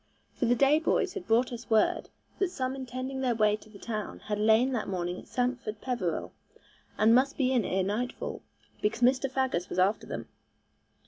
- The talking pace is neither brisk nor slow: Yes, average, 190 wpm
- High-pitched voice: Yes, high, 240 Hz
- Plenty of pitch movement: No, average, 3.5 semitones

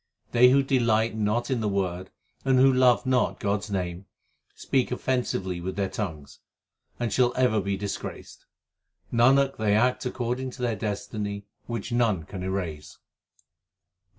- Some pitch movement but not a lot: Yes, average, 4.3 semitones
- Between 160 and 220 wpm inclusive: No, average, 150 wpm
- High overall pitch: No, low, 110 Hz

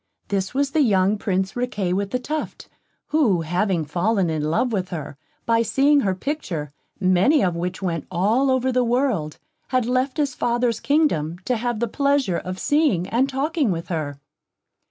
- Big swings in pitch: Yes, wide, 6.5 semitones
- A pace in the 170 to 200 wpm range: Yes, average, 175 wpm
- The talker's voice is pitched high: Yes, high, 215 Hz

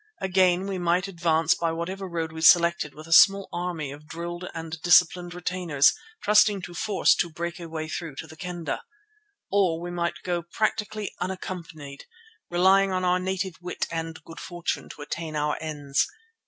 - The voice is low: No, medium, 175 Hz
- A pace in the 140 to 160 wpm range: No, average, 170 wpm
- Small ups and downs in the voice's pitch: Yes, narrow, 2.3 semitones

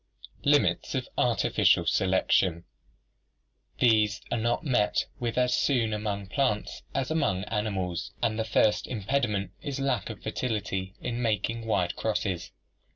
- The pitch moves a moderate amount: Yes, average, 3.5 semitones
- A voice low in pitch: Yes, low, 110 Hz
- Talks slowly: Yes, slow, 130 wpm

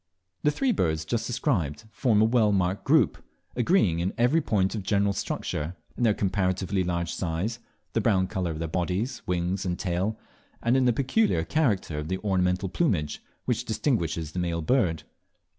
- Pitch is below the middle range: Yes, very low, 95 Hz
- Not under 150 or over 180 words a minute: Yes, average, 175 wpm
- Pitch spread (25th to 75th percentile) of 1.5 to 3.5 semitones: No, average, 4.9 semitones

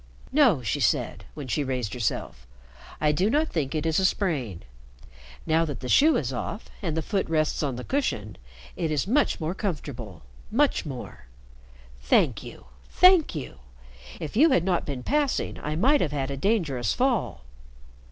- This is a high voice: No, medium, 155 Hz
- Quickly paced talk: No, average, 170 wpm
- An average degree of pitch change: No, wide, 8.4 semitones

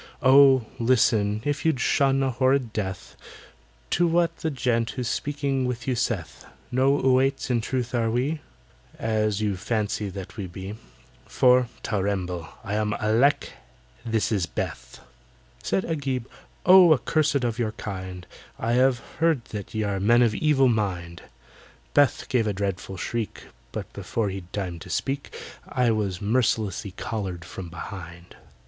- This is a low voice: Yes, low, 115 Hz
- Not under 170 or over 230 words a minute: No, average, 150 wpm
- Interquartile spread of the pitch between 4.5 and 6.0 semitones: Yes, average, 4.8 semitones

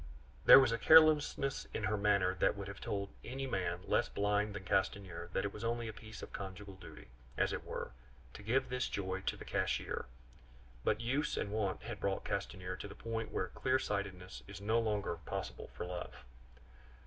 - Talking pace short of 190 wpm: No, average, 195 wpm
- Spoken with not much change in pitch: No, average, 3.1 semitones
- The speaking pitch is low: Yes, low, 100 Hz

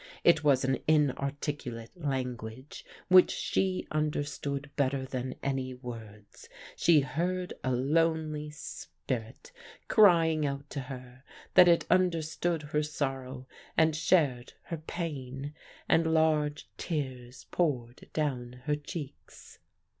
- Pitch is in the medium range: Yes, medium, 145 Hz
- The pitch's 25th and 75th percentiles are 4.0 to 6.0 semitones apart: No, average, 3.6 semitones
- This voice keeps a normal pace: No, slow, 110 wpm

